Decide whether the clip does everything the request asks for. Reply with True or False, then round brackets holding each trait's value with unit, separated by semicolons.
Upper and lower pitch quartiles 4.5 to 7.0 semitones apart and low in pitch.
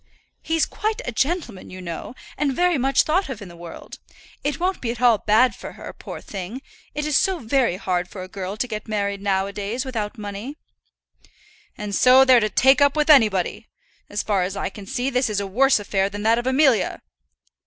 False (5.1 semitones; 230 Hz)